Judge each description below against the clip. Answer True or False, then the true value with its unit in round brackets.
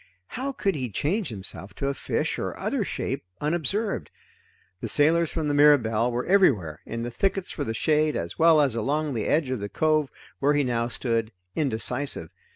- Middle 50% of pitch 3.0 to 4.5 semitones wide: False (5.2 semitones)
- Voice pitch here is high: False (145 Hz)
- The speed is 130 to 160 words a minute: False (185 wpm)